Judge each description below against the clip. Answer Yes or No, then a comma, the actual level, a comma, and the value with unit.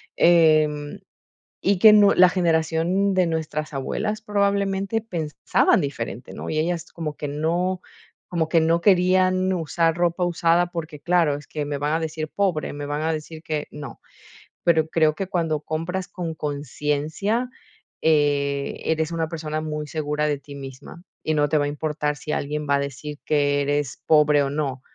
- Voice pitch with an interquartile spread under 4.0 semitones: Yes, average, 2.9 semitones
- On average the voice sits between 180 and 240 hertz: No, medium, 155 Hz